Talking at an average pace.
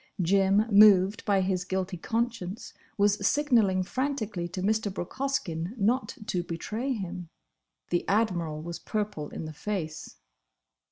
No: slow, 120 wpm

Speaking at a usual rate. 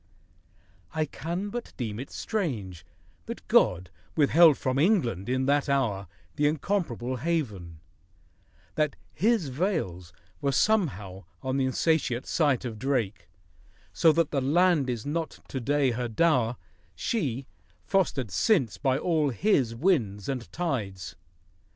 No: slow, 130 wpm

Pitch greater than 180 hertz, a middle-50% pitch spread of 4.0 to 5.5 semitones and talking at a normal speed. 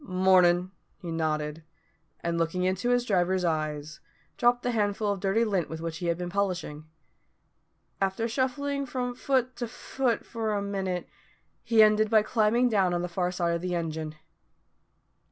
Yes: high, 190 Hz; average, 4.9 semitones; average, 165 wpm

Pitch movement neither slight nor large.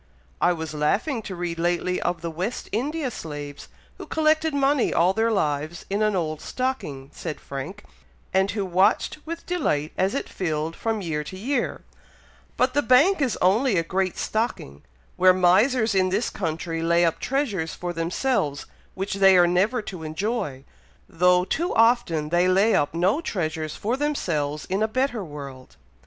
No: wide, 6.0 semitones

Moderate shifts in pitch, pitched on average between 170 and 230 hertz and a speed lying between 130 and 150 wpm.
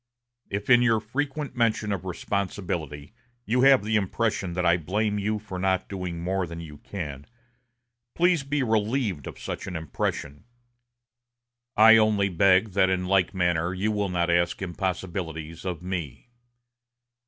No: average, 3.8 semitones; very low, 95 Hz; average, 145 wpm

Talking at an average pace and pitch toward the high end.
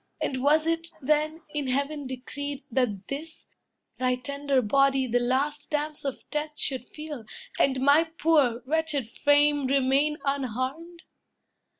No: slow, 130 wpm; very high, 280 Hz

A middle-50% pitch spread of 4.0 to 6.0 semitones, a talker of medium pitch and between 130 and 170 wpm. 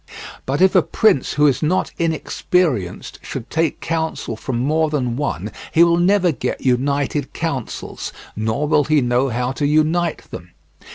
Yes: average, 4.6 semitones; medium, 145 Hz; average, 160 wpm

